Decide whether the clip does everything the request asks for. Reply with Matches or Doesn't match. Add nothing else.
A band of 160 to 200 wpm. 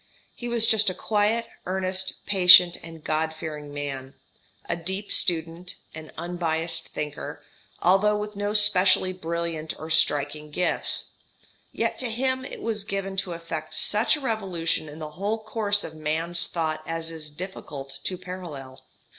Doesn't match